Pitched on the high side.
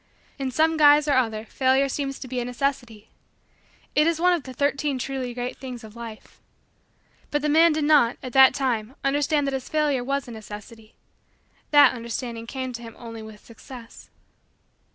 Yes: very high, 260 Hz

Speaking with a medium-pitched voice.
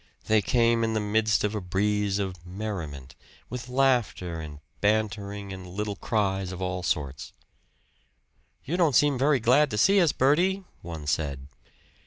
No: low, 105 Hz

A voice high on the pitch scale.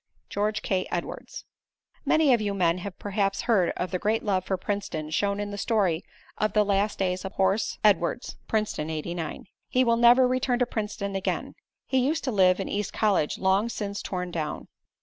Yes: high, 200 Hz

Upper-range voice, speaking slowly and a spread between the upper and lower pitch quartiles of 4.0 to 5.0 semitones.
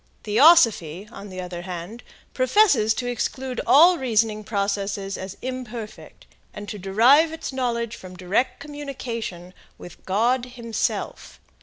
Yes: high, 225 Hz; slow, 125 wpm; average, 4.6 semitones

